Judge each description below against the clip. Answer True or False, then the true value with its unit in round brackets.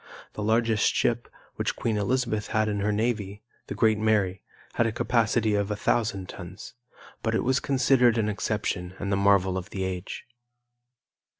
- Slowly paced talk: False (170 wpm)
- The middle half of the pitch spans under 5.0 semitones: True (2.6 semitones)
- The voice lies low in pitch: True (105 Hz)